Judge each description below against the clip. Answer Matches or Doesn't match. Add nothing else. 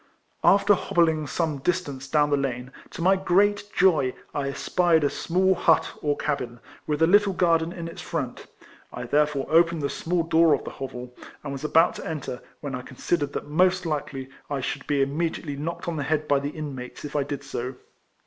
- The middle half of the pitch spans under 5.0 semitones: Matches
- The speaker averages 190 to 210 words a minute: Matches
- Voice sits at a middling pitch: Matches